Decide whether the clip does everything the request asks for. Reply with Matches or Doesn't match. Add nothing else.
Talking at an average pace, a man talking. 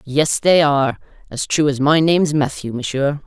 Doesn't match